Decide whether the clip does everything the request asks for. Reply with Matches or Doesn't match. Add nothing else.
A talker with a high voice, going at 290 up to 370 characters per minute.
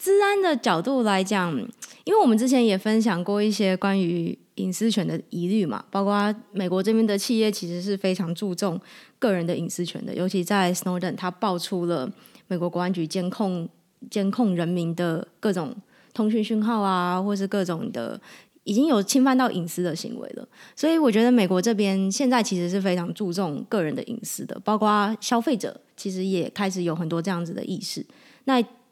Matches